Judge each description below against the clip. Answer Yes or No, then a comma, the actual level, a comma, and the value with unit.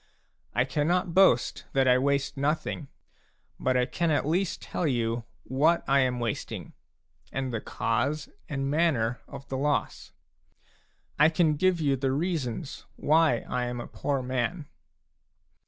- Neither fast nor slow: Yes, average, 145 wpm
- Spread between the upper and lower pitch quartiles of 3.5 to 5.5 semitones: Yes, average, 3.9 semitones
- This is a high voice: No, medium, 140 Hz